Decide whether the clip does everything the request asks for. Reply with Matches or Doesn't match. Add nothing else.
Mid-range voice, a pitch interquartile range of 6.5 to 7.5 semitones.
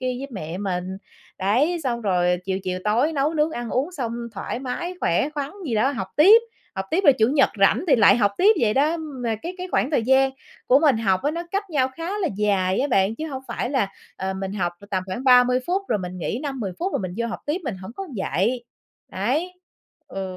Doesn't match